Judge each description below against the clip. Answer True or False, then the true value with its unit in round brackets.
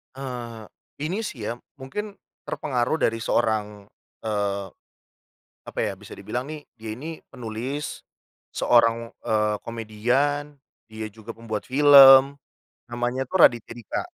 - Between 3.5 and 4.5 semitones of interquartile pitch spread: True (3.8 semitones)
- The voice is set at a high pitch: False (120 Hz)